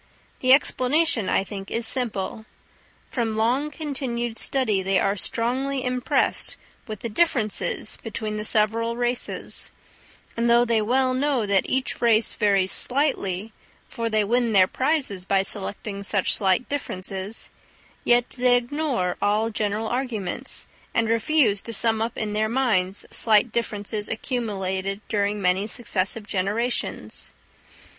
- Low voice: No, high, 225 Hz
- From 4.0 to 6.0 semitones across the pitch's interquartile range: No, average, 3.4 semitones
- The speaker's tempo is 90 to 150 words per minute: Yes, slow, 135 wpm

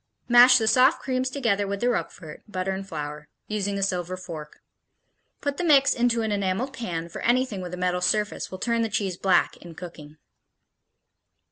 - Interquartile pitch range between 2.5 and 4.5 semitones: No, average, 5.1 semitones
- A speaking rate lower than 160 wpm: No, average, 180 wpm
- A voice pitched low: No, high, 200 Hz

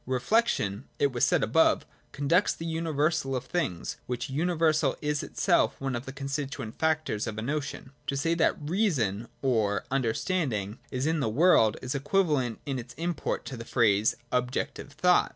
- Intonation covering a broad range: No, average, 4.9 semitones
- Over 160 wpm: Yes, average, 175 wpm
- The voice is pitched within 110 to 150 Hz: Yes, low, 135 Hz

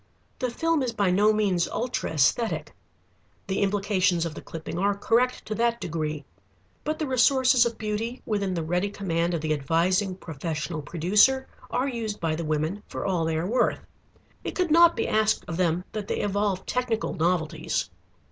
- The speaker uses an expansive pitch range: Yes, wide, 5.7 semitones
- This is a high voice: Yes, high, 200 Hz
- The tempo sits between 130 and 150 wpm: No, average, 175 wpm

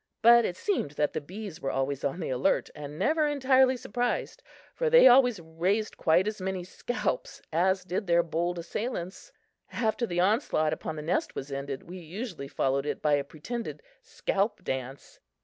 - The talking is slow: No, average, 175 wpm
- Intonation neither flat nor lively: No, wide, 7.6 semitones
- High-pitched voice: No, medium, 180 Hz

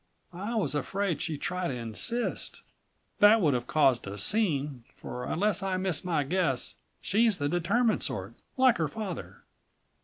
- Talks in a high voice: No, medium, 175 Hz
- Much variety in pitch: Yes, wide, 6.6 semitones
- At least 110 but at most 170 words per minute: Yes, average, 155 wpm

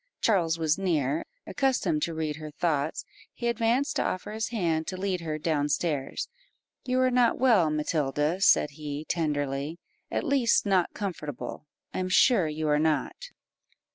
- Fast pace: No, average, 160 wpm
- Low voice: No, medium, 165 Hz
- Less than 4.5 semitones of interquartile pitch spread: No, average, 5.0 semitones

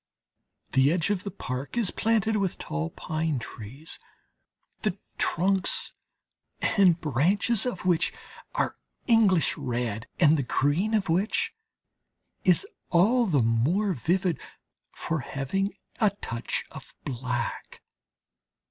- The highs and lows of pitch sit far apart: Yes, wide, 6.9 semitones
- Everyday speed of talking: No, slow, 115 wpm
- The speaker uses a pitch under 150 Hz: No, medium, 170 Hz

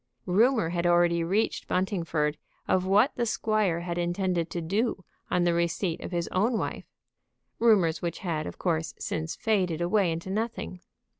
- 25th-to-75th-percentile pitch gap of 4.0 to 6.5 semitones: No, average, 3.1 semitones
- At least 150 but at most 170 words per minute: Yes, average, 160 wpm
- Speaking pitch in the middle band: Yes, medium, 175 Hz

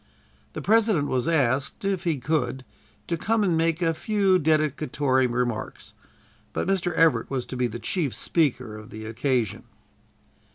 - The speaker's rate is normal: Yes, average, 155 wpm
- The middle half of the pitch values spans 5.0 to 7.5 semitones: Yes, average, 5.3 semitones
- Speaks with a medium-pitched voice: Yes, medium, 150 Hz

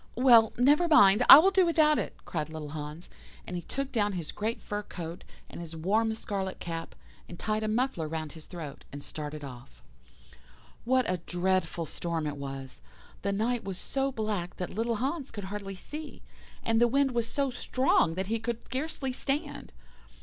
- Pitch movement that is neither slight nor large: No, wide, 7.3 semitones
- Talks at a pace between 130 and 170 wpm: No, average, 185 wpm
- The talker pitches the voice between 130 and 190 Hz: No, high, 205 Hz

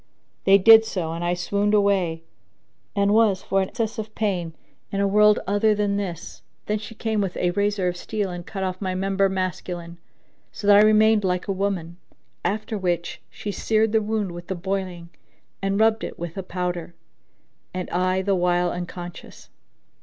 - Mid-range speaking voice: No, high, 195 Hz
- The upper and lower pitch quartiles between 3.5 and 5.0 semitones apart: No, average, 2.8 semitones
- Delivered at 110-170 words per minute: No, average, 180 wpm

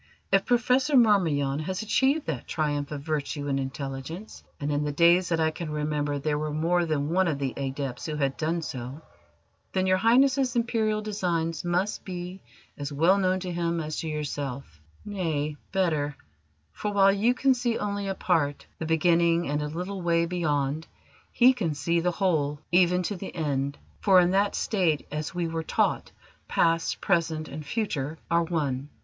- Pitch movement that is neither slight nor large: Yes, average, 4.3 semitones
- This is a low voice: No, medium, 165 Hz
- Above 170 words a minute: Yes, average, 180 wpm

